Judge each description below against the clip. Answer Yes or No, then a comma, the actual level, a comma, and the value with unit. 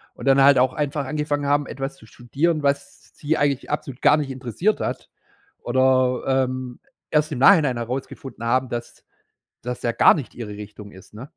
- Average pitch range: Yes, average, 3.0 semitones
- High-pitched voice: No, low, 135 Hz